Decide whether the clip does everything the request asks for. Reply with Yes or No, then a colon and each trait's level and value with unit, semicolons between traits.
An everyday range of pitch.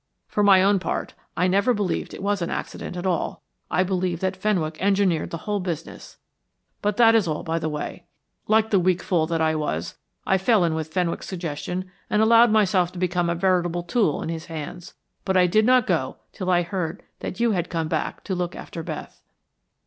Yes: average, 3.2 semitones